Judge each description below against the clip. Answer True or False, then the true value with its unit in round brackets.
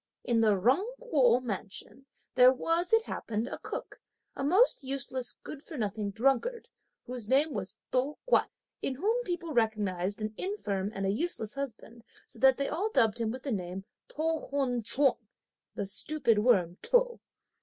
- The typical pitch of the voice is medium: False (255 Hz)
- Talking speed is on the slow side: False (170 wpm)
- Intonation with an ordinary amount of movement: False (6.1 semitones)